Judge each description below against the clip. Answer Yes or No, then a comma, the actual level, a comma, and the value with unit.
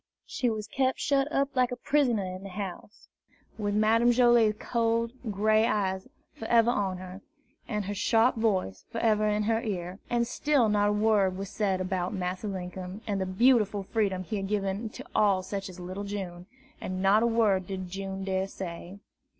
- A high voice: Yes, high, 205 Hz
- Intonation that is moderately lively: Yes, average, 3.1 semitones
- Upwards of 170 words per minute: Yes, average, 185 wpm